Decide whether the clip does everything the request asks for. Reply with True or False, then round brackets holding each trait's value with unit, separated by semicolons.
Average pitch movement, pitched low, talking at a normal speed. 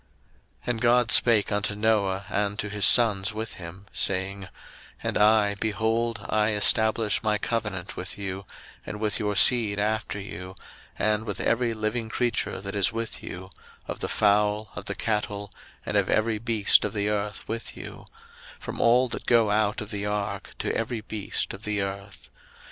False (1.7 semitones; 105 Hz; 180 wpm)